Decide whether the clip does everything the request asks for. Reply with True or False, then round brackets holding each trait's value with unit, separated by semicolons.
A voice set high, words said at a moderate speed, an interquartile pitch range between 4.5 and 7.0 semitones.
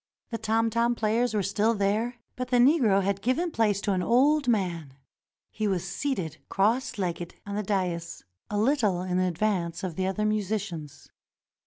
False (205 Hz; 170 wpm; 3.9 semitones)